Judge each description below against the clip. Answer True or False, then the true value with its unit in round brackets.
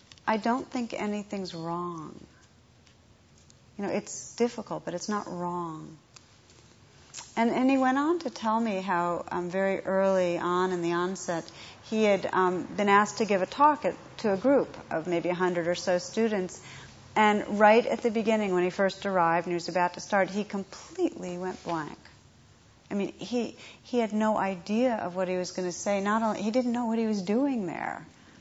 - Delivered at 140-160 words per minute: False (190 wpm)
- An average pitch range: True (3.9 semitones)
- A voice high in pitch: True (195 Hz)